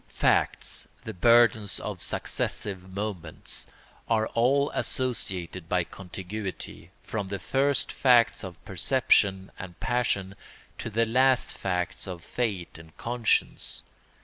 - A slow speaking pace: Yes, slow, 105 wpm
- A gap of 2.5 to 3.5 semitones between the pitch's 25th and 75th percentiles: No, average, 4.6 semitones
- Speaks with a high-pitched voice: No, low, 100 Hz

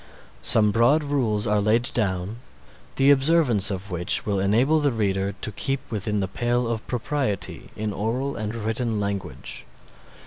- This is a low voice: Yes, low, 110 Hz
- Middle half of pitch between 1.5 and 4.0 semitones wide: Yes, average, 3.7 semitones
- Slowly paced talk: No, average, 150 wpm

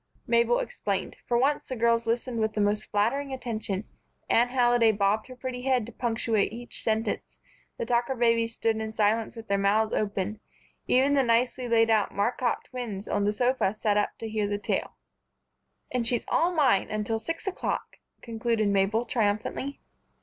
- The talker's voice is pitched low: No, high, 230 Hz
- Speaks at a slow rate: No, average, 170 wpm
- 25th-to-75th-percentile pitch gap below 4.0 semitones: Yes, narrow, 2.4 semitones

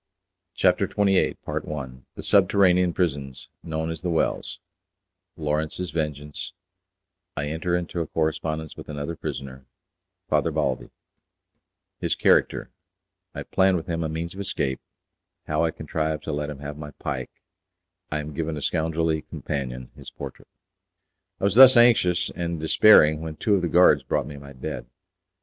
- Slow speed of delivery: No, average, 150 wpm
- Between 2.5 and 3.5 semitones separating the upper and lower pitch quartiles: Yes, average, 3.0 semitones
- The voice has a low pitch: Yes, very low, 80 Hz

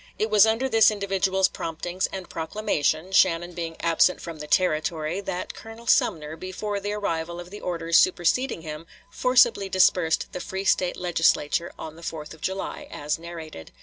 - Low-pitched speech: No, medium, 180 Hz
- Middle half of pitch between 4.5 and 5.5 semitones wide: No, average, 3.3 semitones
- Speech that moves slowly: No, average, 165 wpm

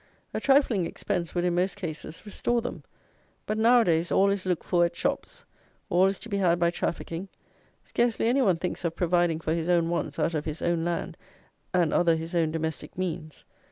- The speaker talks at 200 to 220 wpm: Yes, fast, 205 wpm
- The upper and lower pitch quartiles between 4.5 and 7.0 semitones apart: No, average, 2.8 semitones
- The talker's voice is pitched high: No, medium, 175 Hz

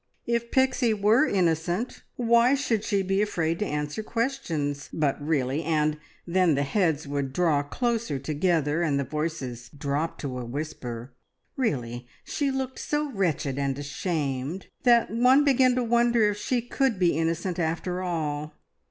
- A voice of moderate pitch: Yes, medium, 170 Hz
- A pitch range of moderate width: No, wide, 8.2 semitones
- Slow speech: No, average, 150 wpm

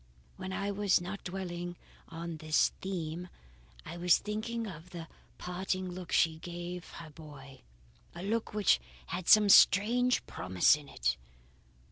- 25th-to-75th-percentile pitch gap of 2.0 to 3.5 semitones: Yes, average, 3.2 semitones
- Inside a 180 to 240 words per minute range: No, average, 140 wpm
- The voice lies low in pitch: No, medium, 180 Hz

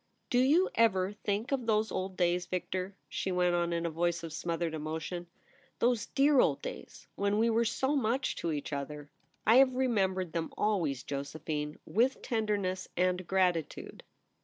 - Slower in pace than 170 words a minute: No, average, 190 wpm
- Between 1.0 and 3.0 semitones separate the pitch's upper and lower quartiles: No, average, 5.2 semitones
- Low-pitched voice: No, medium, 185 Hz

